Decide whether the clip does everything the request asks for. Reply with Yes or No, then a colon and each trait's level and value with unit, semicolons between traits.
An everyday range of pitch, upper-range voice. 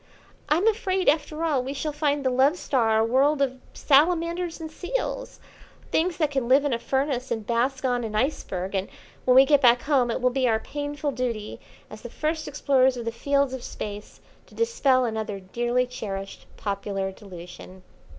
Yes: average, 4.4 semitones; very high, 260 Hz